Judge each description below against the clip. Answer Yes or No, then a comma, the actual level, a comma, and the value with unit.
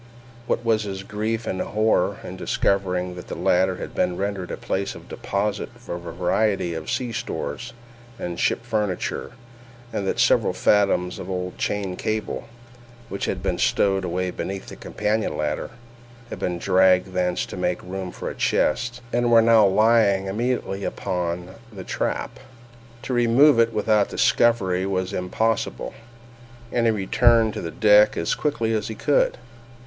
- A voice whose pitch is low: Yes, low, 100 Hz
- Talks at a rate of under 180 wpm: Yes, average, 160 wpm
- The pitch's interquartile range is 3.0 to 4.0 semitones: Yes, average, 3.5 semitones